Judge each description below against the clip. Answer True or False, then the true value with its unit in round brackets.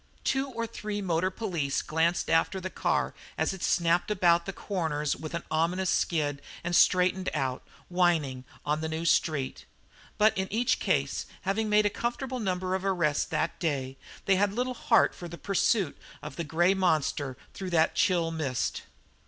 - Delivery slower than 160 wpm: False (170 wpm)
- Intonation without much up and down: False (3.7 semitones)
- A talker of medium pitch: True (175 Hz)